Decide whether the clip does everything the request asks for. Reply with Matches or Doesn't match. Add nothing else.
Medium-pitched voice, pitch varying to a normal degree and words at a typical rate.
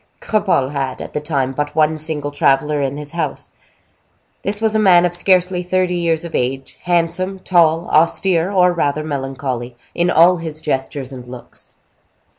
Matches